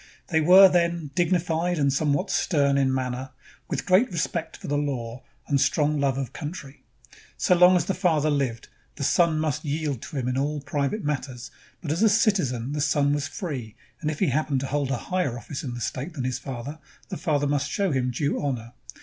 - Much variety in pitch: No, average, 4.0 semitones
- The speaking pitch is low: No, medium, 145 Hz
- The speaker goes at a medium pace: No, fast, 210 wpm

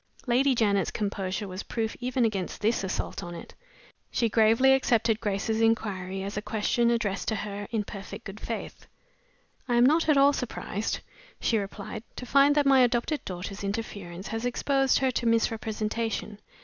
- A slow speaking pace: No, average, 165 wpm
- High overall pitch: Yes, high, 225 Hz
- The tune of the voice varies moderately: Yes, average, 3.4 semitones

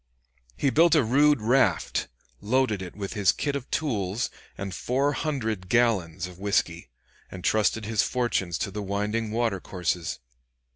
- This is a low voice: Yes, low, 110 Hz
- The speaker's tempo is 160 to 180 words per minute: No, average, 150 wpm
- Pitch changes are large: No, average, 4.9 semitones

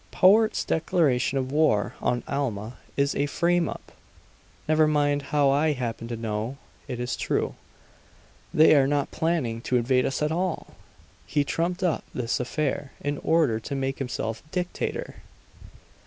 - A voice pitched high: No, medium, 140 Hz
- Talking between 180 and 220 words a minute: No, average, 150 wpm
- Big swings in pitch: No, average, 4.1 semitones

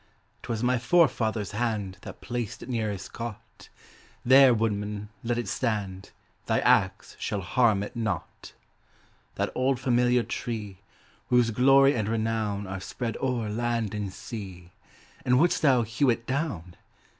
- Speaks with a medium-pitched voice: No, low, 115 Hz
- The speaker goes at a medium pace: Yes, average, 145 wpm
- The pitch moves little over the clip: No, average, 3.2 semitones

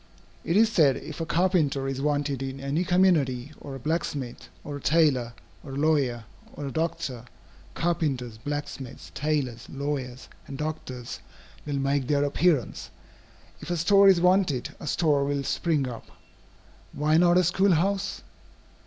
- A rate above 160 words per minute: No, average, 155 wpm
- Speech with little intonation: No, average, 3.8 semitones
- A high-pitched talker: No, medium, 145 Hz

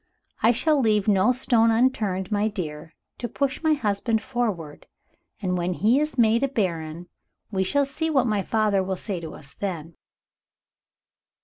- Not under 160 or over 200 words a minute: Yes, average, 165 wpm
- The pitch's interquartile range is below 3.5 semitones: No, average, 5.0 semitones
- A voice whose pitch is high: Yes, high, 210 Hz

